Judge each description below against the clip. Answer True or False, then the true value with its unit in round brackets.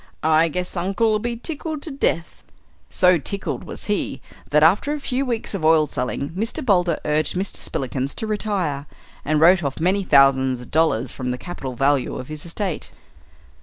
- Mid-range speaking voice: True (165 Hz)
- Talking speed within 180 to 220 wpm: False (170 wpm)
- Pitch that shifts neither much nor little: False (6.3 semitones)